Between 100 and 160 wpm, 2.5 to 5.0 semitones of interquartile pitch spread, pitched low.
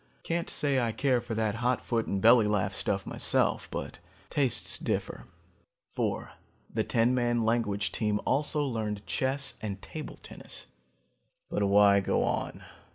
Yes: average, 150 wpm; average, 3.6 semitones; low, 115 Hz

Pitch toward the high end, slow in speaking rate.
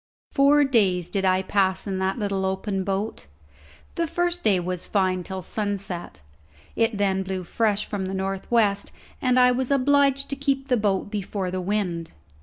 No: high, 200 Hz; average, 175 wpm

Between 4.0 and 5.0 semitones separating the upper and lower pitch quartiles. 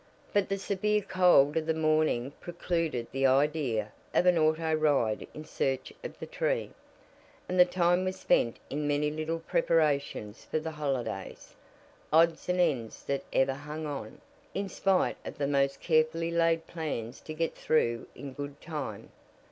No: average, 3.4 semitones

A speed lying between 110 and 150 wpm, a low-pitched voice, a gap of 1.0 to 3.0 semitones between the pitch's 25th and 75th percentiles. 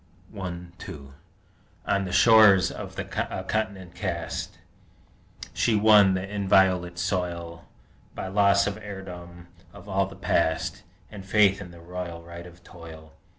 Yes: slow, 135 wpm; very low, 95 Hz; narrow, 2.4 semitones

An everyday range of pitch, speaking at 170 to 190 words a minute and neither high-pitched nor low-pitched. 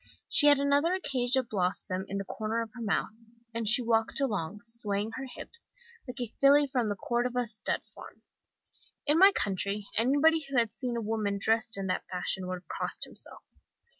No: average, 4.6 semitones; average, 185 wpm; high, 230 Hz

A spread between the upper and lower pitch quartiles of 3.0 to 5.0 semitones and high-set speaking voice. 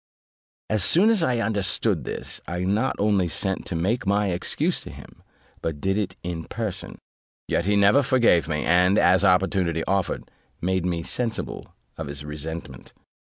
No: average, 3.7 semitones; very low, 95 Hz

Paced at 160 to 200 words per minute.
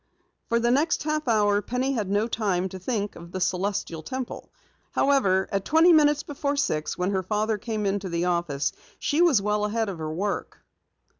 Yes: average, 190 wpm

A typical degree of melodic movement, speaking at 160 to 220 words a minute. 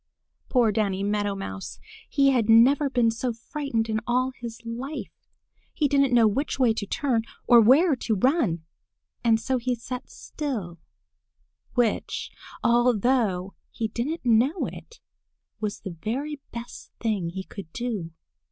No: average, 3.7 semitones; average, 145 wpm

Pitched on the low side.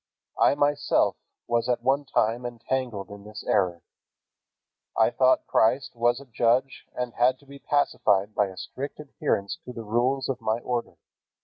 Yes: low, 120 Hz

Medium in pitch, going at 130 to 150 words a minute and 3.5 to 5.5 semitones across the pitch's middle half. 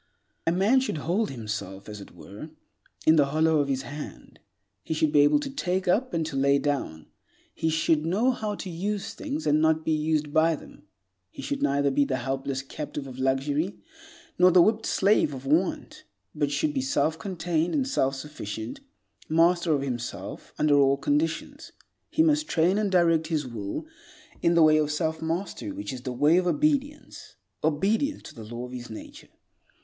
No: medium, 155 Hz; average, 185 wpm; average, 5.1 semitones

